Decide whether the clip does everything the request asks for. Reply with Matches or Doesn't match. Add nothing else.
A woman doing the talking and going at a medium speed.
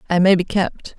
Doesn't match